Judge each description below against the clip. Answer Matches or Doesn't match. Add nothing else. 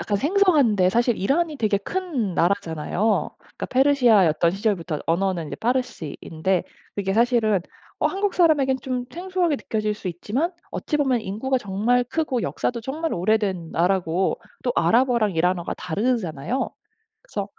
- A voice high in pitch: Matches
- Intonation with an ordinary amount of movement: Doesn't match